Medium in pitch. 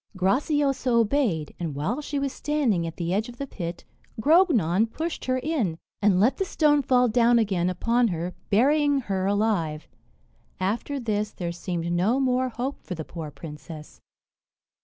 No: high, 220 Hz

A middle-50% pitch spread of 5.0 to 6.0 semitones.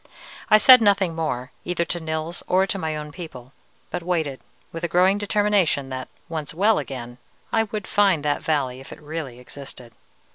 Yes: average, 5.3 semitones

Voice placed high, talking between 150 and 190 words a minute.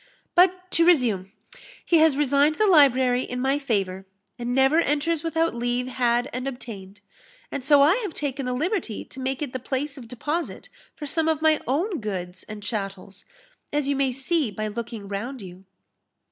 Yes: very high, 265 Hz; average, 180 wpm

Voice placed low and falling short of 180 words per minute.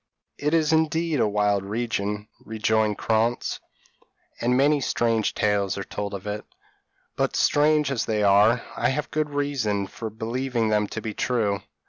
Yes: low, 110 Hz; average, 160 wpm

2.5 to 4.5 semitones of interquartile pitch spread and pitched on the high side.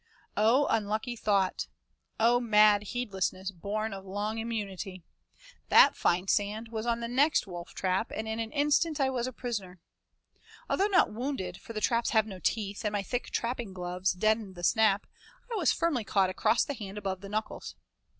Yes: average, 3.4 semitones; high, 215 Hz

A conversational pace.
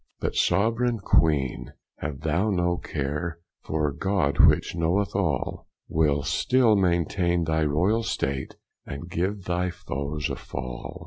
No: slow, 130 wpm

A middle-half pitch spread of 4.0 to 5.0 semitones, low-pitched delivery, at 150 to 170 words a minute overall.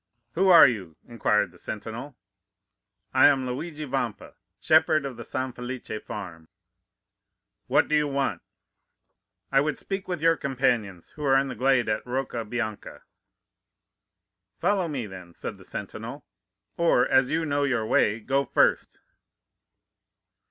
No: average, 4.5 semitones; low, 130 Hz; average, 140 wpm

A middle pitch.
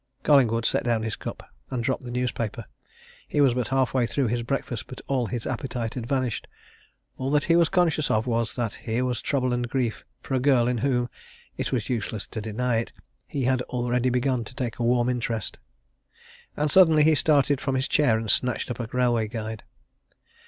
No: low, 125 Hz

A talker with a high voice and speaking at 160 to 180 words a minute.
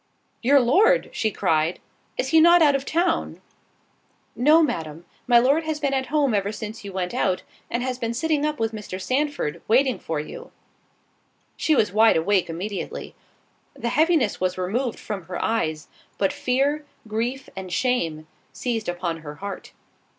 Yes: high, 230 Hz; average, 165 wpm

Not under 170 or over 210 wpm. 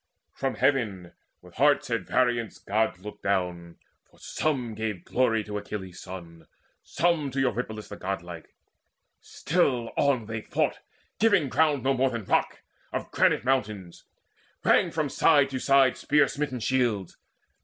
No: average, 145 wpm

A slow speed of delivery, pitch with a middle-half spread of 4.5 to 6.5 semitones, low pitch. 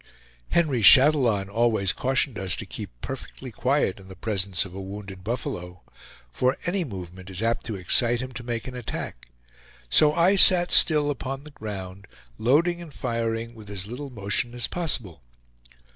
No: average, 165 wpm; wide, 5.6 semitones; low, 115 Hz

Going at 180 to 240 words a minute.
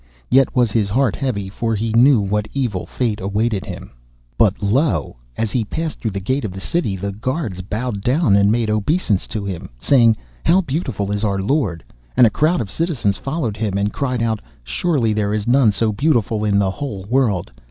Yes: average, 200 wpm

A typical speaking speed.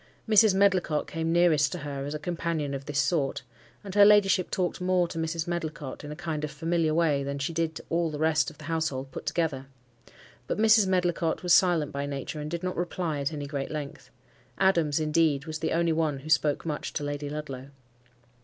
No: fast, 210 wpm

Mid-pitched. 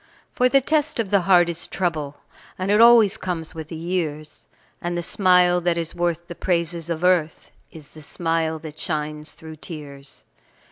Yes: medium, 170 Hz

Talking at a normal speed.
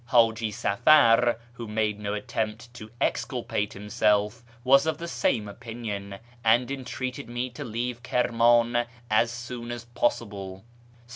No: slow, 130 wpm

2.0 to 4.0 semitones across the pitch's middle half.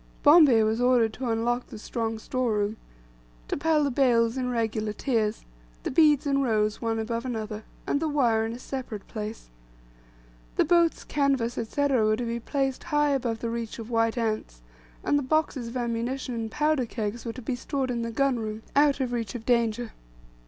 Yes: average, 3.2 semitones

